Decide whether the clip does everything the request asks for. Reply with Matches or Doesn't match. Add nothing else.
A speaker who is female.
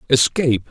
Doesn't match